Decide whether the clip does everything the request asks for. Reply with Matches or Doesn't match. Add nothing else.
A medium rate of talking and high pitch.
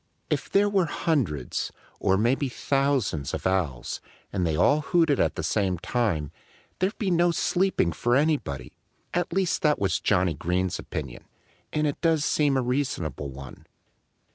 Doesn't match